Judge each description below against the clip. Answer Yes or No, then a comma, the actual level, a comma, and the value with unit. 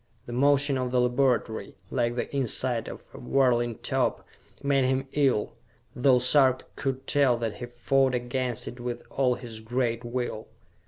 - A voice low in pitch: Yes, low, 125 Hz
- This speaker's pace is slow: No, average, 160 wpm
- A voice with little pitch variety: Yes, narrow, 1.9 semitones